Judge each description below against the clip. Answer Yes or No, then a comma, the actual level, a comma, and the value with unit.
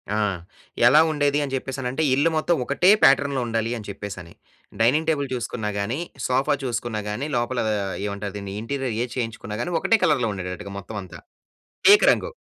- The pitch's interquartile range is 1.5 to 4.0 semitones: No, average, 5.1 semitones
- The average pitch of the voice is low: Yes, low, 125 Hz